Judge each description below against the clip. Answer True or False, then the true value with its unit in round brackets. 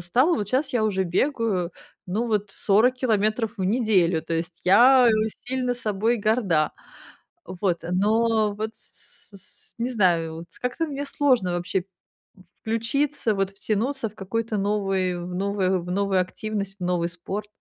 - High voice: True (205 Hz)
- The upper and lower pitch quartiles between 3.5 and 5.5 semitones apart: True (4.0 semitones)